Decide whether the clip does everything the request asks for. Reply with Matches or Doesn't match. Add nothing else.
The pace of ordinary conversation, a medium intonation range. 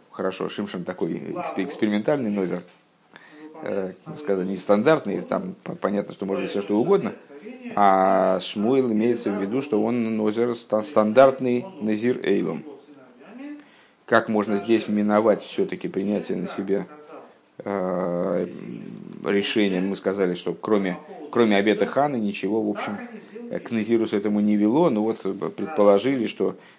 Matches